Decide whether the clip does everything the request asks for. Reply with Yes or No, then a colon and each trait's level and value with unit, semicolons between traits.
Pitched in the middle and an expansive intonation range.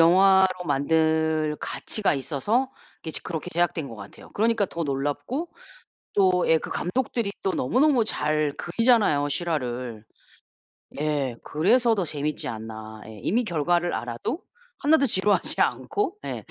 Yes: medium, 170 Hz; wide, 6.6 semitones